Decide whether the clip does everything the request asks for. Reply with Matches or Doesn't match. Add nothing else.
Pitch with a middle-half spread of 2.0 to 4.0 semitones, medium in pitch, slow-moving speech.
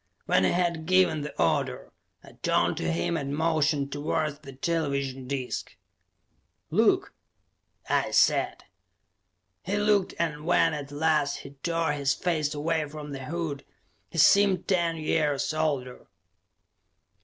Matches